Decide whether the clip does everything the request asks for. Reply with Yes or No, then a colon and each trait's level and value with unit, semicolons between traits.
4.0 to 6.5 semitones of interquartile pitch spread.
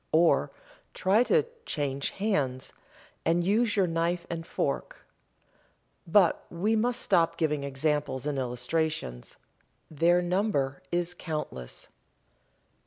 Yes: average, 4.6 semitones